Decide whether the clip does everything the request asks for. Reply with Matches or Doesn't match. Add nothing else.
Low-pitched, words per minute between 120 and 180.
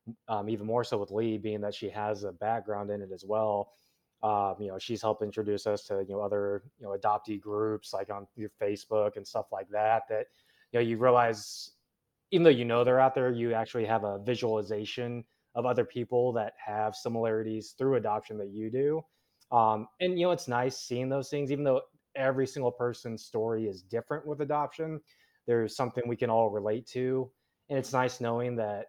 Doesn't match